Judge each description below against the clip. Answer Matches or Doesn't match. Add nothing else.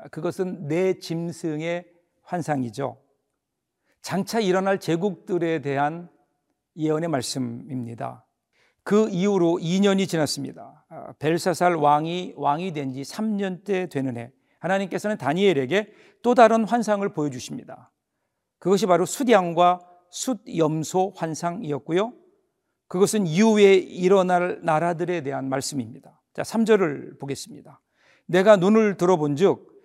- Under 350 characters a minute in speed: Matches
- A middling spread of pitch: Matches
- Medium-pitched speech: Matches